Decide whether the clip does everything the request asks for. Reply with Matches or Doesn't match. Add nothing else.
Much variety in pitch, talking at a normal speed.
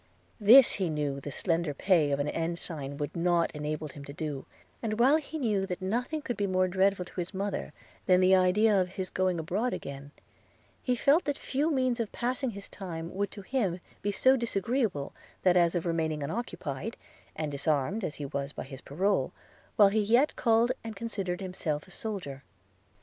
Matches